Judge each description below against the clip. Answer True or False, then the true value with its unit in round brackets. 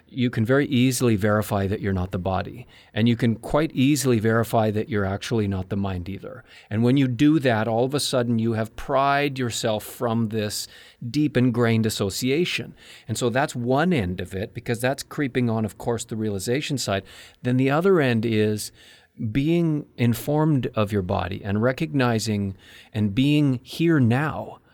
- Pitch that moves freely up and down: False (3.8 semitones)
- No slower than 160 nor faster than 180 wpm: True (175 wpm)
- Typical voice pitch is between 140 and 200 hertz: False (120 Hz)